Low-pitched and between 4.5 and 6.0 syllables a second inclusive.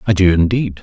Yes: very low, 95 Hz; 5.8 syllables/s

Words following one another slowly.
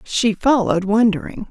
Yes: slow, 120 wpm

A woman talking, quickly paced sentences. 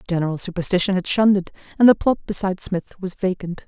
No: female; average, 195 wpm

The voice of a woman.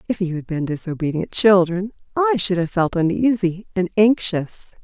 Yes: female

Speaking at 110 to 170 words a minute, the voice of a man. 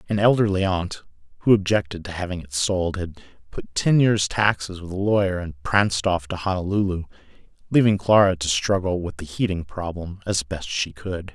No: average, 180 wpm; male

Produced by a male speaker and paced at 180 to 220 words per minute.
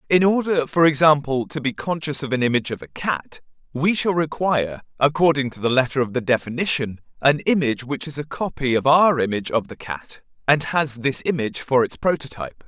Yes: male; average, 200 wpm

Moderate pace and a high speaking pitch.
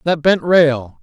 No: average, 175 wpm; medium, 155 Hz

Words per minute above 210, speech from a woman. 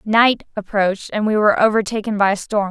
No: average, 200 wpm; female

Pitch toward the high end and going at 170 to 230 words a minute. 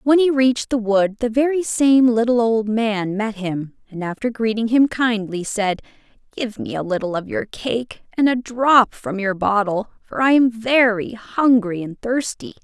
Yes: high, 225 Hz; average, 185 wpm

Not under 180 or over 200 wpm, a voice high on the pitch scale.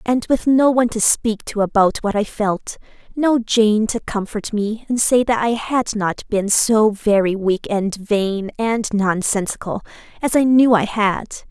Yes: average, 185 wpm; high, 215 Hz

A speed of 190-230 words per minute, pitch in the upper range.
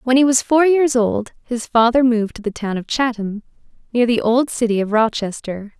Yes: fast, 205 wpm; high, 235 Hz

